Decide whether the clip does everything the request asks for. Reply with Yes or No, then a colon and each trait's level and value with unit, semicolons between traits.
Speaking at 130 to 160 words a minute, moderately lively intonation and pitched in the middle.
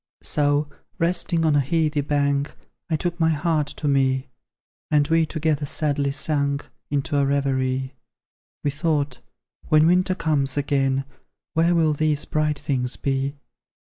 No: average, 140 wpm; narrow, 2.1 semitones; medium, 145 Hz